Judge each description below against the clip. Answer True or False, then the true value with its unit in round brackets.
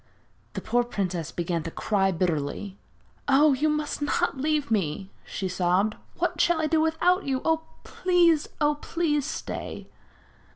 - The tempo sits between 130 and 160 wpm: True (140 wpm)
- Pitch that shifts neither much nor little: False (8.6 semitones)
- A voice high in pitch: True (265 Hz)